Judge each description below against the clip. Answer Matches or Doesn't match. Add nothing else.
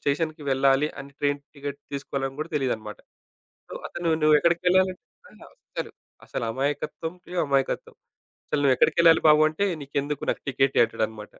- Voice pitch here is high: Doesn't match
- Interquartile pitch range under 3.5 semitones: Matches